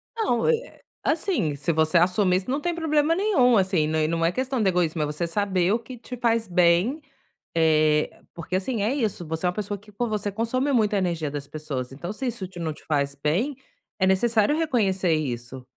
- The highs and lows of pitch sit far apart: Yes, wide, 7.0 semitones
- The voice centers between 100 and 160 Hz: No, high, 190 Hz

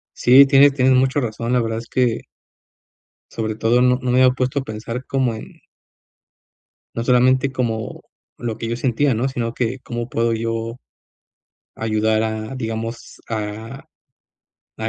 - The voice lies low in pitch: Yes, low, 120 Hz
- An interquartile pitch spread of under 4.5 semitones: Yes, narrow, 2.4 semitones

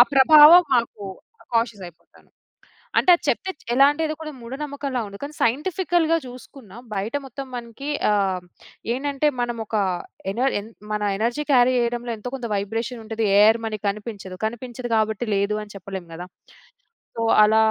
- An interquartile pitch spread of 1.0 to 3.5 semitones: No, average, 4.4 semitones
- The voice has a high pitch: Yes, high, 235 Hz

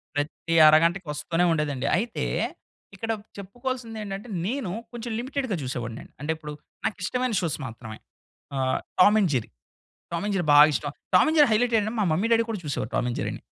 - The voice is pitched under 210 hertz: Yes, medium, 185 Hz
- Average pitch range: No, wide, 7.4 semitones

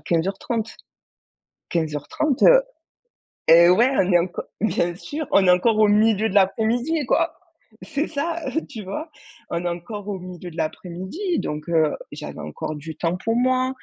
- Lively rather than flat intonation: Yes, wide, 6.7 semitones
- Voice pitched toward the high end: Yes, high, 200 Hz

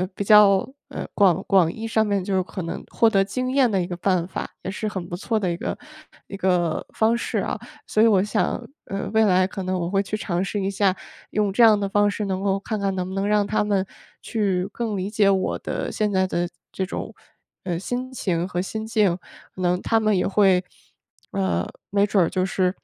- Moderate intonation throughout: No, narrow, 2.3 semitones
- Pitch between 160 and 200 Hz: Yes, high, 195 Hz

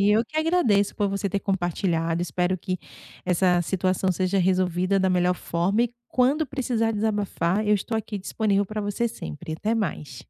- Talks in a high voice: Yes, high, 195 Hz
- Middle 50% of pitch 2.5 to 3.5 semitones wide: Yes, average, 3.2 semitones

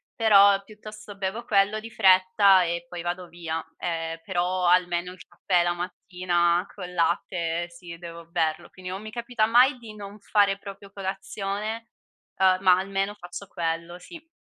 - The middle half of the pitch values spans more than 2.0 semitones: Yes, average, 2.7 semitones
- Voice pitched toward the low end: No, medium, 185 Hz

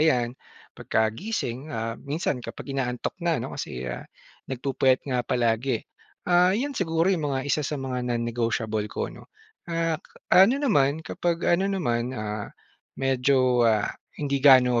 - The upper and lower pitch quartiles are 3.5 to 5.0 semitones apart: No, wide, 5.4 semitones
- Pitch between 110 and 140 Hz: Yes, low, 135 Hz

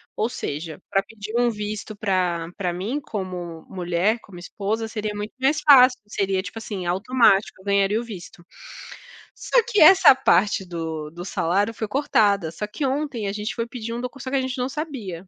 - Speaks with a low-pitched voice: No, high, 210 Hz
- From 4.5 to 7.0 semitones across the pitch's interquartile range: Yes, average, 4.8 semitones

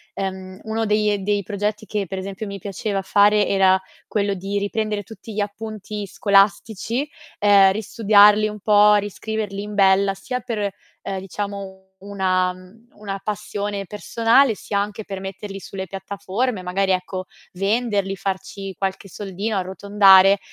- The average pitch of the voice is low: No, high, 200 Hz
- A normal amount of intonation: No, narrow, 1.5 semitones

